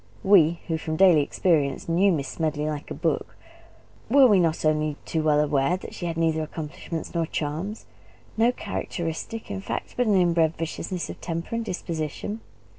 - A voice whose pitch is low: No, medium, 165 Hz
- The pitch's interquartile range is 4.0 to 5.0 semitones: No, average, 3.3 semitones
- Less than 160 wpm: No, average, 175 wpm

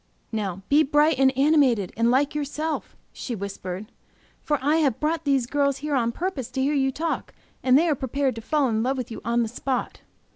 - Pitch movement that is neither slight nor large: Yes, average, 4.0 semitones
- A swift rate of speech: Yes, fast, 210 wpm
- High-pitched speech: Yes, very high, 270 Hz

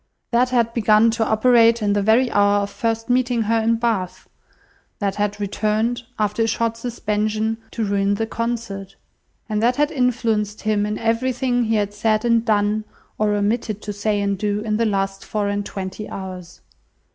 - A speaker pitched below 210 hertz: No, high, 215 Hz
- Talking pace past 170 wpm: Yes, average, 180 wpm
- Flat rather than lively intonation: Yes, narrow, 2.1 semitones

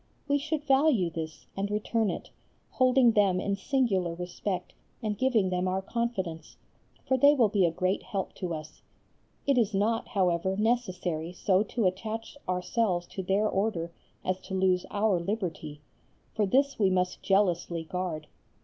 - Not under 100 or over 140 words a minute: No, average, 160 wpm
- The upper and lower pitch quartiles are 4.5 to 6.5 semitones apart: No, average, 3.9 semitones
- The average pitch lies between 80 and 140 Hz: No, high, 195 Hz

